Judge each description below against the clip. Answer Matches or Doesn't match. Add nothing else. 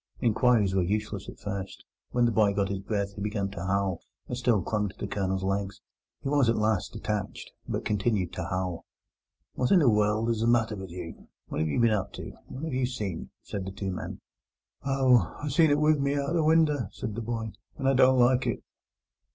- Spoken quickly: Matches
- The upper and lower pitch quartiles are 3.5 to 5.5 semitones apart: Matches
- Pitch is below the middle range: Matches